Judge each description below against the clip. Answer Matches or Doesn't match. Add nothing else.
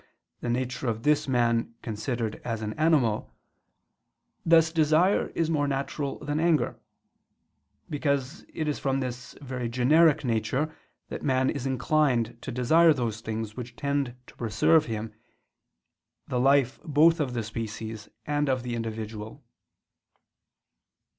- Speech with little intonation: Doesn't match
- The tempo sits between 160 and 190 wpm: Doesn't match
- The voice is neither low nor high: Doesn't match